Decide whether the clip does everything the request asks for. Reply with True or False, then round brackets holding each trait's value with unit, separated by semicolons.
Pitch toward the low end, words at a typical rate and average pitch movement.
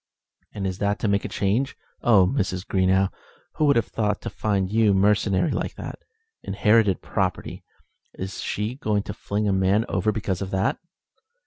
False (100 Hz; 175 wpm; 2.1 semitones)